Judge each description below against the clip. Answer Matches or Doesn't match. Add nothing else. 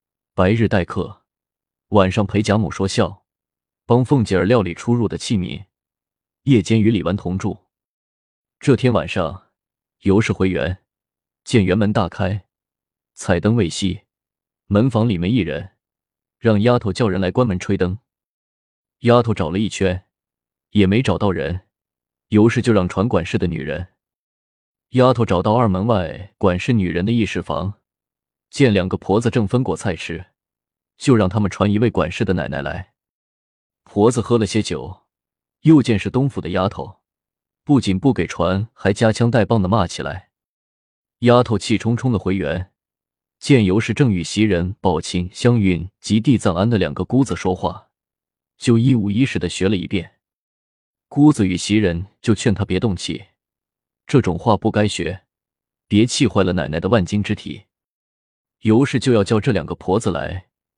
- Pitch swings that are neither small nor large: Matches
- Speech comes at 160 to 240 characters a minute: Matches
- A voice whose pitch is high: Doesn't match